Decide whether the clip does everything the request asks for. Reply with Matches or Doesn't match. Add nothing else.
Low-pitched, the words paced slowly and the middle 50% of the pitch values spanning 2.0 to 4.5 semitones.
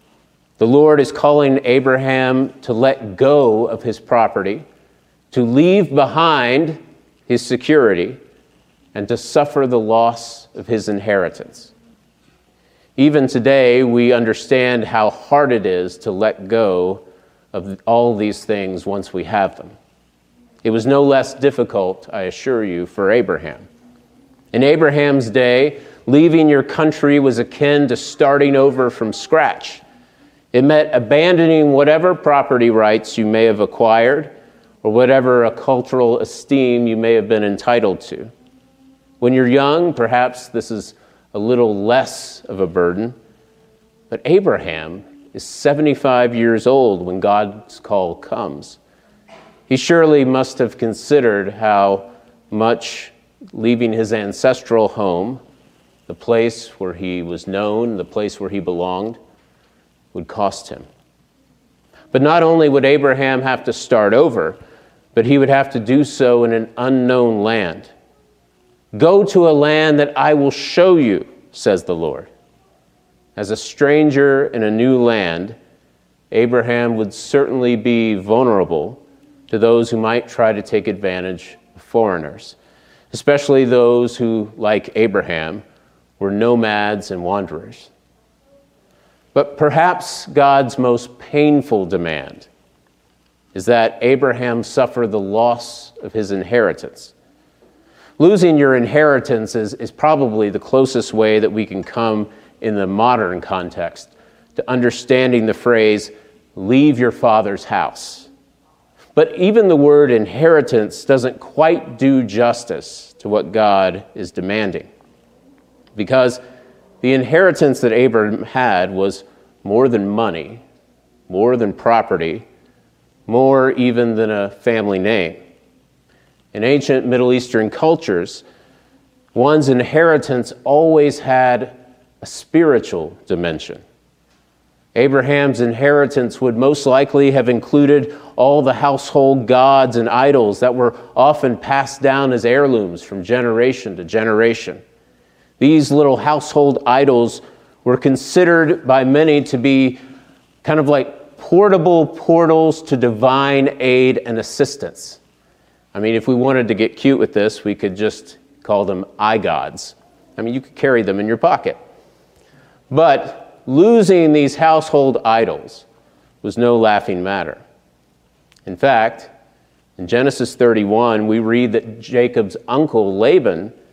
Matches